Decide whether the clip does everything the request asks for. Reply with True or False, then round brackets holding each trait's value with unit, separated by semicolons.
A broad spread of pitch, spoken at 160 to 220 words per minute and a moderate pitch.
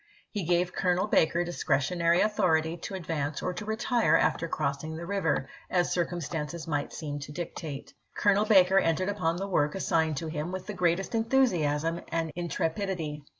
False (3.1 semitones; 165 wpm; 170 Hz)